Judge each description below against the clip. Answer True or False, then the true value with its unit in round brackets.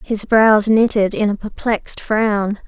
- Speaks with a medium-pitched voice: False (210 Hz)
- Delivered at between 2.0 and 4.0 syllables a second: True (3.9 syllables/s)